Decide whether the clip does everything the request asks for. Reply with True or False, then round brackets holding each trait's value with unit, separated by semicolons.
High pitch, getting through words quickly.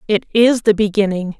False (210 Hz; 170 wpm)